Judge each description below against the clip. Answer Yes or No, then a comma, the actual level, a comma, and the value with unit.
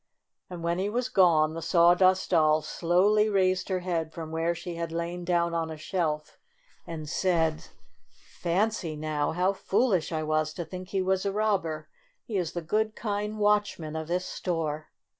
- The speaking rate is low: No, average, 175 wpm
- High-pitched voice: No, medium, 175 Hz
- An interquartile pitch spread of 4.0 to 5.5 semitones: No, average, 3.1 semitones